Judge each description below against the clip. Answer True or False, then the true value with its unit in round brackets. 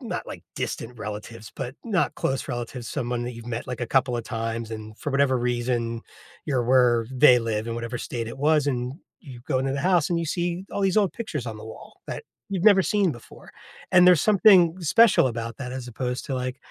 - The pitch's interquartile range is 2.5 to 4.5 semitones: False (5.3 semitones)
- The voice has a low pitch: True (125 Hz)